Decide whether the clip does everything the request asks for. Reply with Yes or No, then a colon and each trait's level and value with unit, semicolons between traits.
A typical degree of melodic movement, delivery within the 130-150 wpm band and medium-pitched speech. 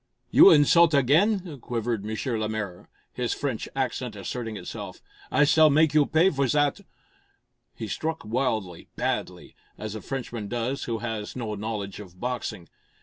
No: average, 5.0 semitones; average, 145 wpm; low, 120 Hz